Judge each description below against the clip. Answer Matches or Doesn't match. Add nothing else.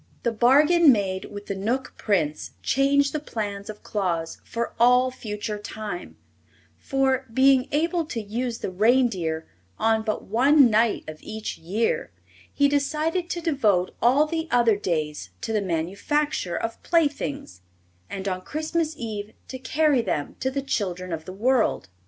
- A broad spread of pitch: Matches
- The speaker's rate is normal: Matches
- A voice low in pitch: Doesn't match